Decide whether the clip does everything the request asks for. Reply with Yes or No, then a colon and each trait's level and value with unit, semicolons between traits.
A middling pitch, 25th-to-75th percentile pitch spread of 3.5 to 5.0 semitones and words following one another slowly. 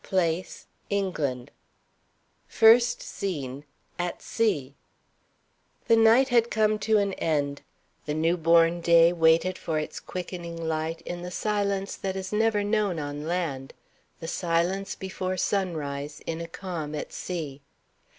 Yes: medium, 175 Hz; average, 3.8 semitones; slow, 130 wpm